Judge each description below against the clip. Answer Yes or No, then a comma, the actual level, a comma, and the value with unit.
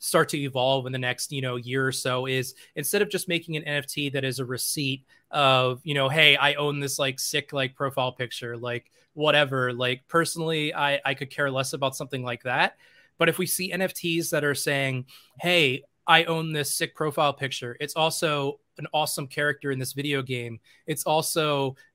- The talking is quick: Yes, fast, 200 wpm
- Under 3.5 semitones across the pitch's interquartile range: Yes, average, 2.9 semitones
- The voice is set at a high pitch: No, medium, 140 Hz